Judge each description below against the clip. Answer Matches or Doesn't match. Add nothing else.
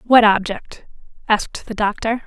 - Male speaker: Doesn't match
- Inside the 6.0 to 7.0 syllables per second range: Doesn't match